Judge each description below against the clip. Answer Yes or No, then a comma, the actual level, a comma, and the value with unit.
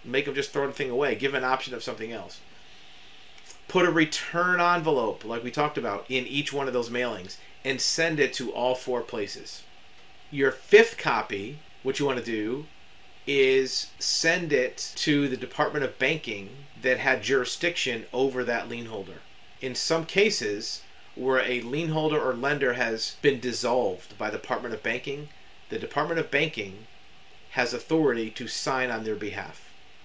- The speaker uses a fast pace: No, average, 170 wpm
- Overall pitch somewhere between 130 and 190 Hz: Yes, low, 135 Hz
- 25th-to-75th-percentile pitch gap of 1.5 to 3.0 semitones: No, average, 3.6 semitones